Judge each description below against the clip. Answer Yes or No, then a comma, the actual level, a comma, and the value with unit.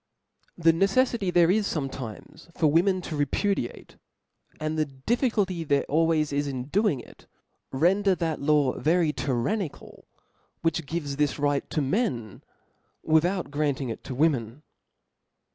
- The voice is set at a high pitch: No, medium, 155 Hz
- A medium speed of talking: No, slow, 130 wpm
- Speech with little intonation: No, average, 4.4 semitones